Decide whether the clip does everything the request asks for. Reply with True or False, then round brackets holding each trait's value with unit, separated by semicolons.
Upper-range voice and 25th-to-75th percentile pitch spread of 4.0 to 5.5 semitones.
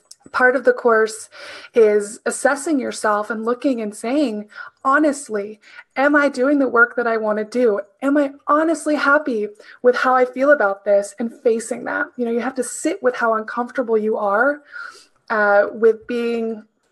True (245 Hz; 4.6 semitones)